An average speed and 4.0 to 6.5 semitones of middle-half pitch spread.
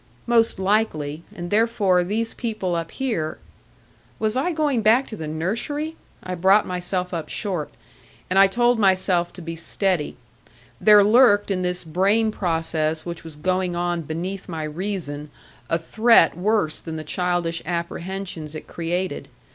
Yes: average, 150 wpm; average, 4.3 semitones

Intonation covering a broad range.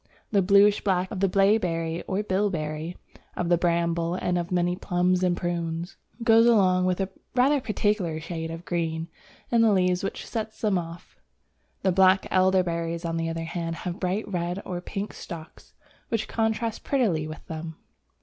No: average, 3.0 semitones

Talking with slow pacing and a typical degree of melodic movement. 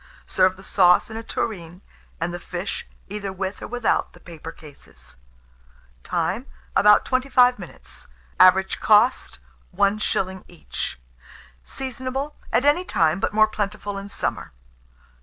Yes: slow, 130 wpm; average, 4.1 semitones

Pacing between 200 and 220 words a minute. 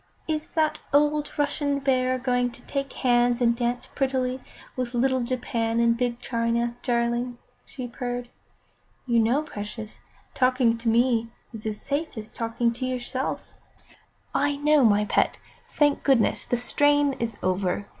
No: average, 145 wpm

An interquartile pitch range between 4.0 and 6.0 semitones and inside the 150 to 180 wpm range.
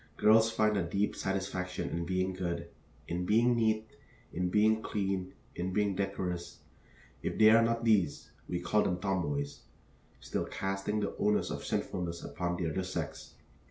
No: average, 3.2 semitones; average, 160 wpm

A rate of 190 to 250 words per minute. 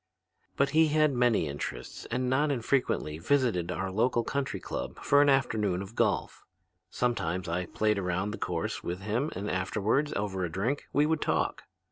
No: average, 170 wpm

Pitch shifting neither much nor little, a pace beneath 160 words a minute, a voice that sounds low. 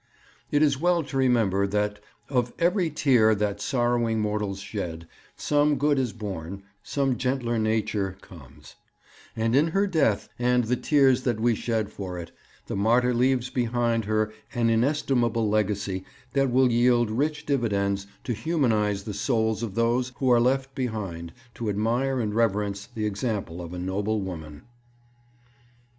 Yes: average, 3.7 semitones; average, 150 wpm; low, 115 Hz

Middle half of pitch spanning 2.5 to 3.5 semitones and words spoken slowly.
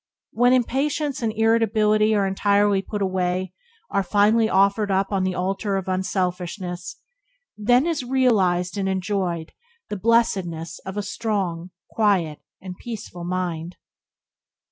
Yes: average, 3.2 semitones; slow, 125 wpm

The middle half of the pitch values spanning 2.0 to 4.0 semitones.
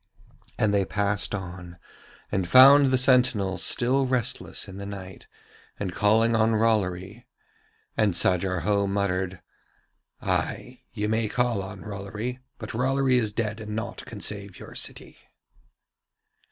Yes: average, 3.2 semitones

